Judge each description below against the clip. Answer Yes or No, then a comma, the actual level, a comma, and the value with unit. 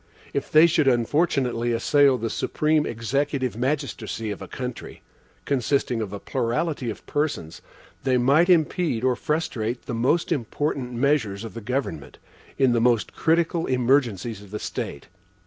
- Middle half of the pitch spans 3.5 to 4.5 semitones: Yes, average, 4.2 semitones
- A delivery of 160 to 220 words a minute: No, average, 145 wpm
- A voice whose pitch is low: Yes, low, 125 Hz